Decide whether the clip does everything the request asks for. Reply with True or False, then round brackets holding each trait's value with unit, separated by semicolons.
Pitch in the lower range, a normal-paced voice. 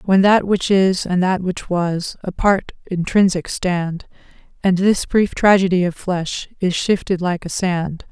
False (185 Hz; 165 wpm)